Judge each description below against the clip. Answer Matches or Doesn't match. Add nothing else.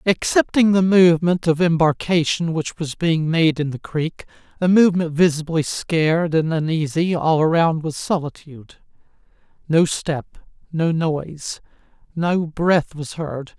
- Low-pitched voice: Doesn't match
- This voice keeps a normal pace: Doesn't match